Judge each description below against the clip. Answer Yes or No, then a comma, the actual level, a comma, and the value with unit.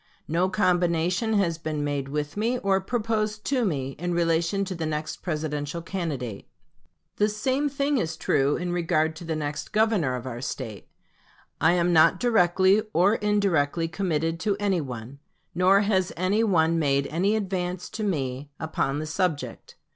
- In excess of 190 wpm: No, average, 160 wpm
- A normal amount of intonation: Yes, average, 4.7 semitones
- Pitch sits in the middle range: Yes, medium, 170 Hz